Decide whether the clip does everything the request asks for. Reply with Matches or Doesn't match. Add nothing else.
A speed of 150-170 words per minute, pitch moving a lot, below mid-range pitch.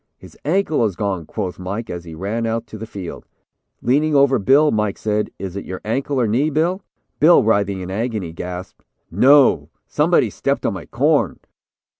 Doesn't match